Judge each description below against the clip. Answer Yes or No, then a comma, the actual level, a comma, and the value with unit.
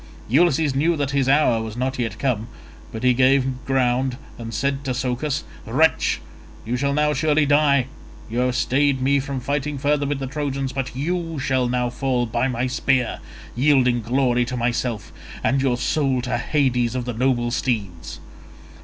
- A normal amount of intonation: No, narrow, 2.3 semitones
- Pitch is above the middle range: No, low, 130 Hz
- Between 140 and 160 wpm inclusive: No, average, 170 wpm